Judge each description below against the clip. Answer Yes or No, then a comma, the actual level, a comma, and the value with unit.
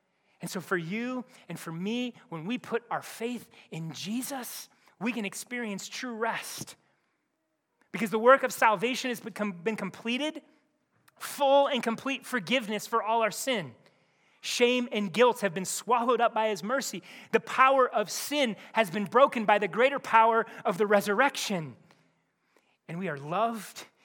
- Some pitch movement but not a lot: Yes, average, 3.7 semitones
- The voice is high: Yes, high, 230 Hz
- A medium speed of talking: Yes, average, 155 wpm